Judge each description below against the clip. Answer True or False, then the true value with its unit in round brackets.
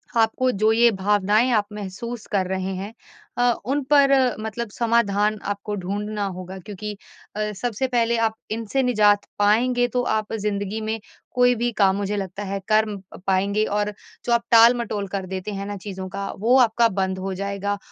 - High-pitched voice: True (210 Hz)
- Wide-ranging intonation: False (2.9 semitones)